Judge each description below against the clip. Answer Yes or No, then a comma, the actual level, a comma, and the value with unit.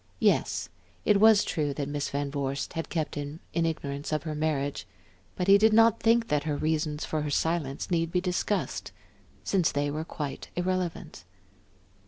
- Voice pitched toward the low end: No, medium, 155 Hz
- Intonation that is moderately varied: Yes, average, 3.9 semitones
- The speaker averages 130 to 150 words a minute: No, average, 175 wpm